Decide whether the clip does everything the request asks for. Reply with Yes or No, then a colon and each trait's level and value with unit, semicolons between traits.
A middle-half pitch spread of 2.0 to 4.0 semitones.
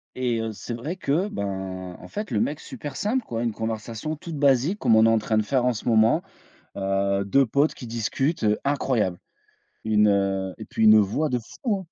No: average, 5.2 semitones